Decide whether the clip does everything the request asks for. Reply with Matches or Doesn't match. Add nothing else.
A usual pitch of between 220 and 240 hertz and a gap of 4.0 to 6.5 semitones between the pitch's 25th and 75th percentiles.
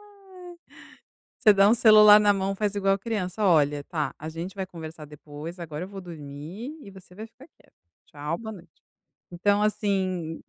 Doesn't match